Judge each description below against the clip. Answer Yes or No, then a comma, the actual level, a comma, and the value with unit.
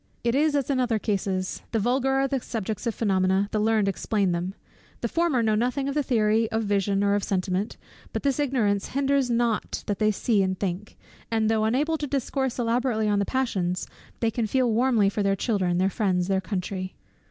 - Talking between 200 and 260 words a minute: Yes, fast, 205 wpm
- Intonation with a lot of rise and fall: No, average, 4.2 semitones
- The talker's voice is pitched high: Yes, high, 220 Hz